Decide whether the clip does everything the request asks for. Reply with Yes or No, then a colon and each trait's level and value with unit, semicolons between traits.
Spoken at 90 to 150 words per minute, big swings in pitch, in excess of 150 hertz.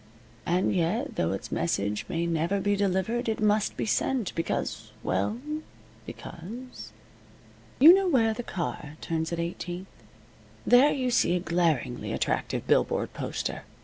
Yes: average, 140 wpm; wide, 5.7 semitones; medium, 185 Hz